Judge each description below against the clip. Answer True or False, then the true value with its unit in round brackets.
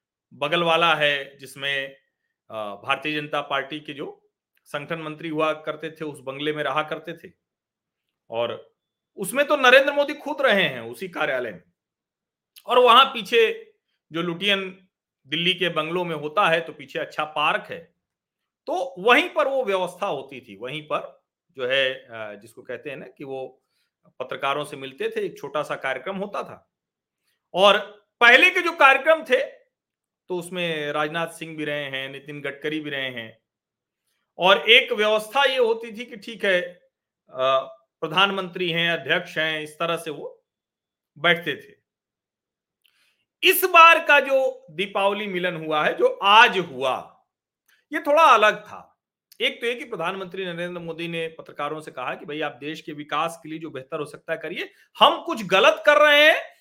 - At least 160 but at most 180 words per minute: True (165 wpm)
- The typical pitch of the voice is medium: True (170 Hz)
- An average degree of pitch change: False (8.1 semitones)